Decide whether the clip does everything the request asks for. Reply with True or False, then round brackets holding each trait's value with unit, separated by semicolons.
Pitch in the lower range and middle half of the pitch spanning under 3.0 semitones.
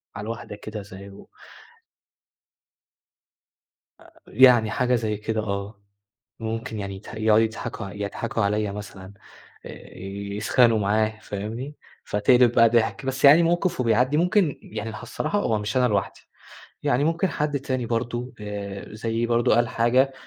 False (115 Hz; 3.3 semitones)